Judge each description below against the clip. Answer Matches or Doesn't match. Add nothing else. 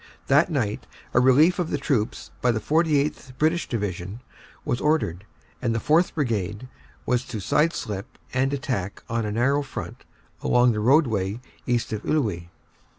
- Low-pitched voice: Matches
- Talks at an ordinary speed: Matches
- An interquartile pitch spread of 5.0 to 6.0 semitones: Matches